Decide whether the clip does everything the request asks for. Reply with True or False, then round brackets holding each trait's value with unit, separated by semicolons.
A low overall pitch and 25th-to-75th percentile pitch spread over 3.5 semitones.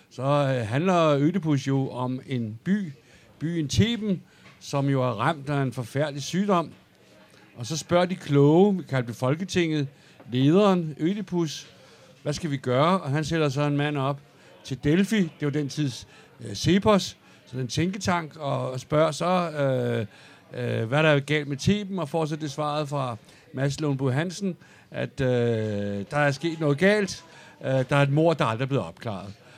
False (145 Hz; 4.1 semitones)